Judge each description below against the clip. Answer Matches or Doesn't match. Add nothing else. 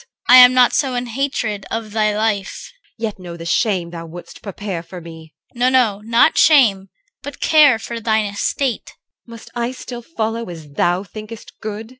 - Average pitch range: Matches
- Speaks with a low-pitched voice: Doesn't match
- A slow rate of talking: Doesn't match